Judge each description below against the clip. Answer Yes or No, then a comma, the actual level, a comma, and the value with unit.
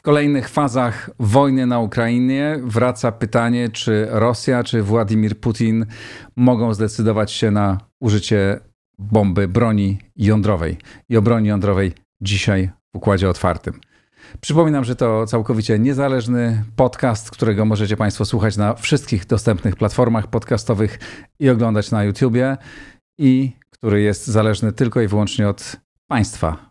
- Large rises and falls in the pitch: No, average, 2.8 semitones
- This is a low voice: Yes, low, 115 Hz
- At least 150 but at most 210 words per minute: No, average, 130 wpm